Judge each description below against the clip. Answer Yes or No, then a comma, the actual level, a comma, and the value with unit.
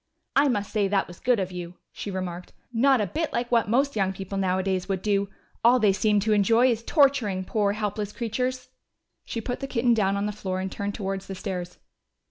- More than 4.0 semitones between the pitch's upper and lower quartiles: No, average, 3.6 semitones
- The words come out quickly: Yes, fast, 215 wpm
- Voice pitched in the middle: No, high, 205 Hz